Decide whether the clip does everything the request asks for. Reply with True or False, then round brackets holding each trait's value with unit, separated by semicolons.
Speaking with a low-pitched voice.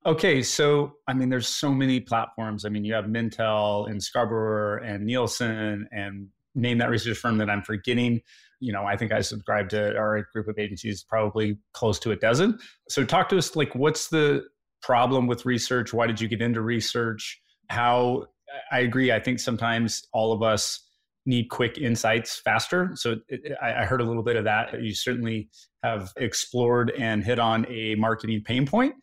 True (115 Hz)